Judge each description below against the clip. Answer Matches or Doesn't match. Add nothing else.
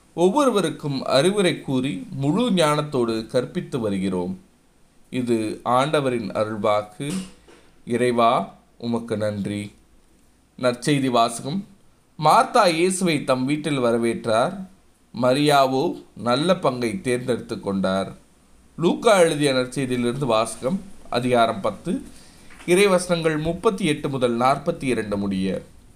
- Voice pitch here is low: Matches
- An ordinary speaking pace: Matches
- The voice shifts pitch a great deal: Matches